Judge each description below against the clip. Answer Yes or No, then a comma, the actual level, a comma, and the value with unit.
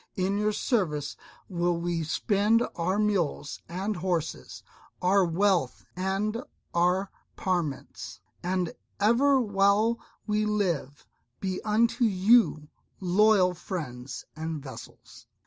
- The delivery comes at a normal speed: No, slow, 105 wpm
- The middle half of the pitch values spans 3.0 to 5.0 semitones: Yes, average, 3.8 semitones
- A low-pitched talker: No, medium, 185 Hz